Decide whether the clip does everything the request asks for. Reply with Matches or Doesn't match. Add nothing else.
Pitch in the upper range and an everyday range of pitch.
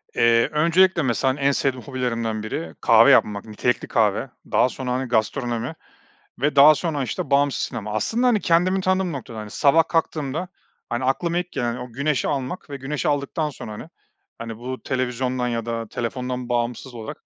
Doesn't match